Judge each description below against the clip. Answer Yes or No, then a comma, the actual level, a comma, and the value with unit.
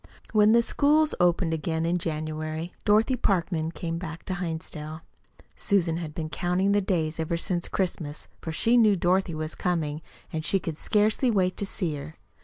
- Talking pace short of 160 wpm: No, average, 175 wpm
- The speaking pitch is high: No, medium, 170 Hz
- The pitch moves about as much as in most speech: Yes, average, 3.6 semitones